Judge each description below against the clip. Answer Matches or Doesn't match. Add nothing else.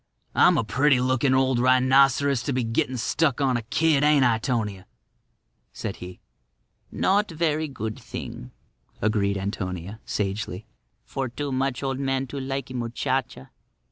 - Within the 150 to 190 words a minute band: Doesn't match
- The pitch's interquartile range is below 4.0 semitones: Matches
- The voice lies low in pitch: Matches